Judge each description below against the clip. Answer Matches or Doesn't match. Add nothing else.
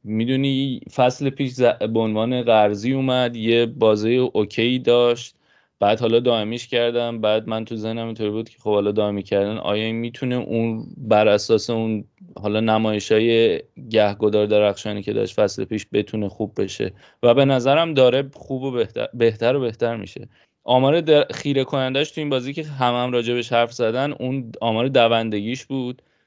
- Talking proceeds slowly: Doesn't match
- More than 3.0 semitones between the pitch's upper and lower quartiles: Doesn't match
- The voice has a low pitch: Matches